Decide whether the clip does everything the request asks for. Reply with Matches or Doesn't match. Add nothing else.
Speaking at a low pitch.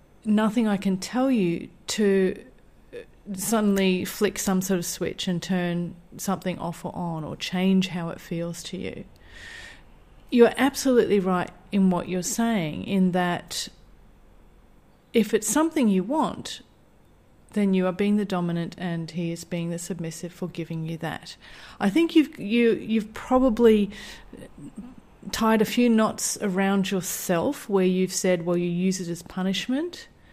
Doesn't match